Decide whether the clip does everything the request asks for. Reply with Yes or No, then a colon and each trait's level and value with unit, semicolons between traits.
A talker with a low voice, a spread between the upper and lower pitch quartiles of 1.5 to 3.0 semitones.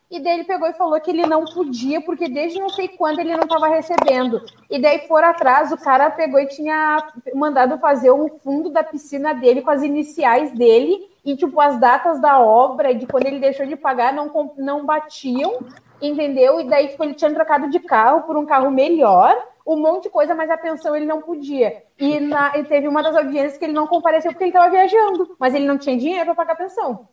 No: very high, 305 Hz; average, 2.7 semitones